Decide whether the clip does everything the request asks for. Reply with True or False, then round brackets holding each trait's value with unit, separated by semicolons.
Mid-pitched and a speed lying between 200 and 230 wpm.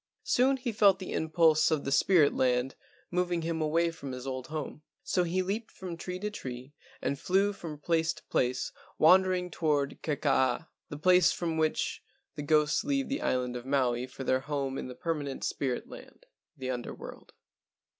False (155 Hz; 180 wpm)